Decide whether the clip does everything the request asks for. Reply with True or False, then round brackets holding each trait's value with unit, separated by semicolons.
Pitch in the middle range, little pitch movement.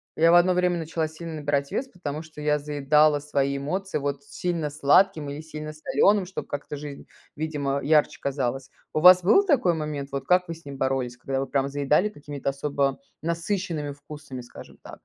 False (150 Hz; 3.0 semitones)